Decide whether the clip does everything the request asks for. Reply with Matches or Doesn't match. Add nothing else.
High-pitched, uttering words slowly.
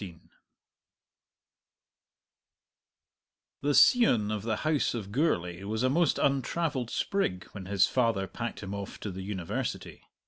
Doesn't match